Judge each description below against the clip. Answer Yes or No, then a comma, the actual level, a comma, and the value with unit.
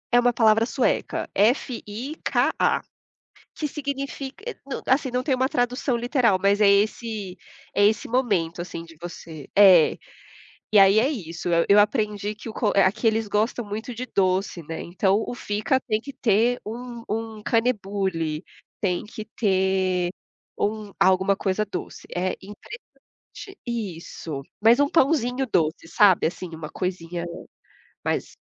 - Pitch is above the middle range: Yes, high, 210 Hz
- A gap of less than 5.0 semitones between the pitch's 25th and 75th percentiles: Yes, average, 4.4 semitones